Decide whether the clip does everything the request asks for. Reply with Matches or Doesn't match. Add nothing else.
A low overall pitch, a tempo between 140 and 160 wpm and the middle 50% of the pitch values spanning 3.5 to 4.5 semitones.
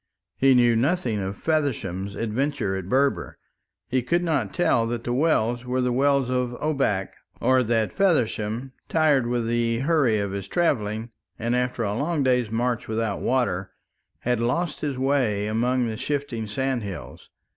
Matches